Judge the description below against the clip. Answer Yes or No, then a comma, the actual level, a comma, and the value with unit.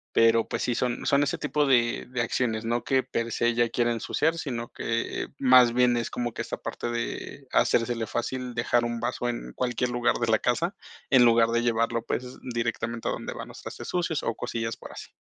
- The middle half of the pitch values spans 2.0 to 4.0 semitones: No, narrow, 1.3 semitones